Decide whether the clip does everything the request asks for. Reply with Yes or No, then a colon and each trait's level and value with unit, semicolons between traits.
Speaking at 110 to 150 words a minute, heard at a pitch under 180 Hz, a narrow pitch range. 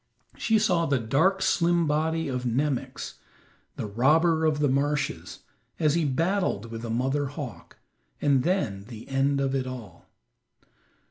No: average, 145 wpm; medium, 140 Hz; average, 4.3 semitones